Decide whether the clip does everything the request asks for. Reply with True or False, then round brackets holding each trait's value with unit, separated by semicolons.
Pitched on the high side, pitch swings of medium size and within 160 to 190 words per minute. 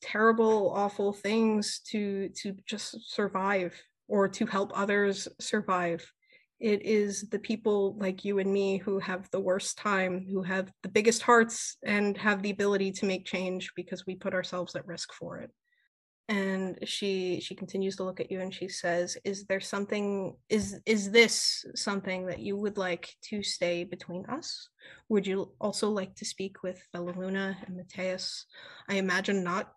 False (195 Hz; 2.0 semitones; 170 wpm)